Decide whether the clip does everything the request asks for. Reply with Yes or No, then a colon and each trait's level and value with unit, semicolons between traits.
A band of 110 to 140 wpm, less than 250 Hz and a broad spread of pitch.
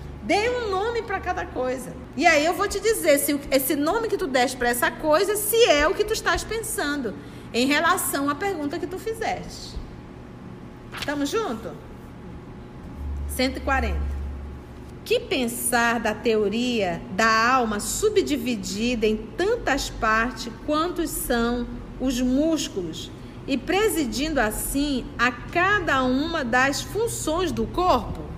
No: average, 130 wpm; very high, 290 Hz; wide, 7.3 semitones